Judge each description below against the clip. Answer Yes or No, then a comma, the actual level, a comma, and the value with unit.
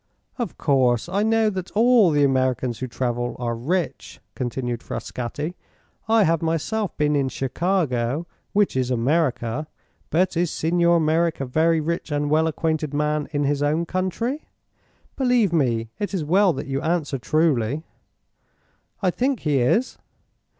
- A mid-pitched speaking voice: Yes, medium, 155 Hz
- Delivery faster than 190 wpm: No, average, 150 wpm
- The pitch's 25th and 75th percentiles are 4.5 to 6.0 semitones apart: Yes, average, 5.2 semitones